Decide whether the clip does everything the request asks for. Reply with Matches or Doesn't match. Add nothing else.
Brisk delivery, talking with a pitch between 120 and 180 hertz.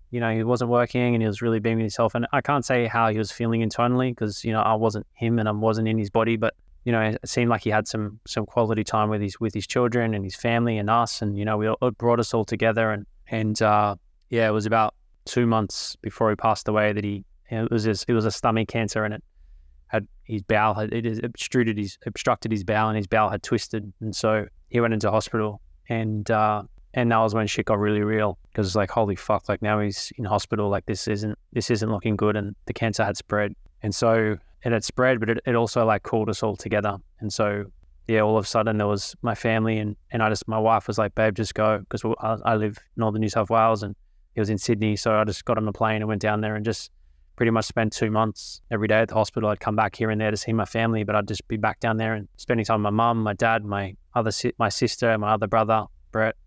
Doesn't match